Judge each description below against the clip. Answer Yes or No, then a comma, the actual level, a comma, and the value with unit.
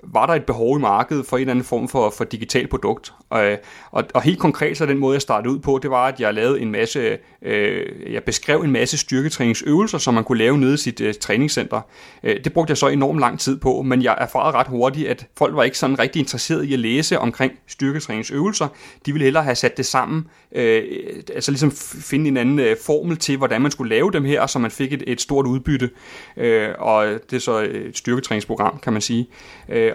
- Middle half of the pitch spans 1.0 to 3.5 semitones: Yes, average, 3.1 semitones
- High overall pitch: No, low, 135 Hz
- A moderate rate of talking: No, fast, 230 wpm